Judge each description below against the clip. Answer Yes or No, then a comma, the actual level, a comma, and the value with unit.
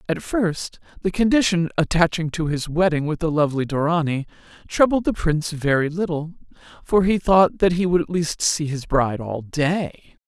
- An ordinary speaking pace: Yes, average, 175 wpm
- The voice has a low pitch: No, medium, 165 Hz